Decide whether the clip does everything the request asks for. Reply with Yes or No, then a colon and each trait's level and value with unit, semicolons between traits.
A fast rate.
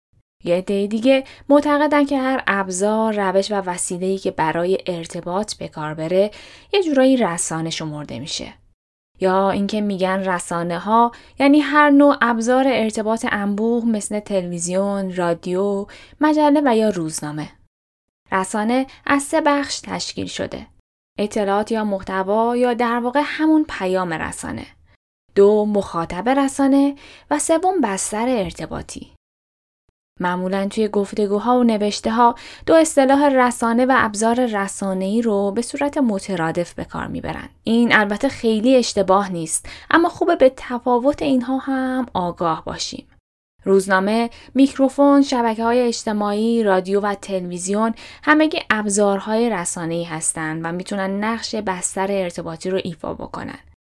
No: average, 125 wpm